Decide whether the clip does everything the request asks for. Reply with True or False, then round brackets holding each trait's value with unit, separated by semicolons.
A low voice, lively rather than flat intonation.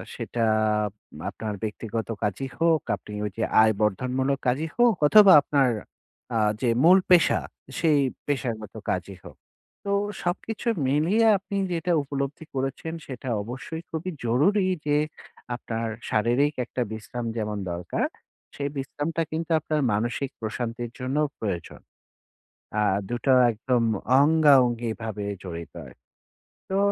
True (130 Hz; 5.8 semitones)